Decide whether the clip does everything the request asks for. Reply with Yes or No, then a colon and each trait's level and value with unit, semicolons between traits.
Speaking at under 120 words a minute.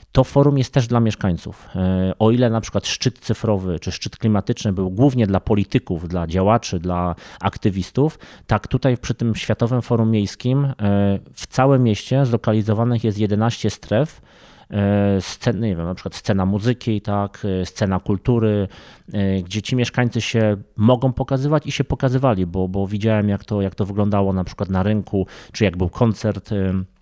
No: fast, 160 wpm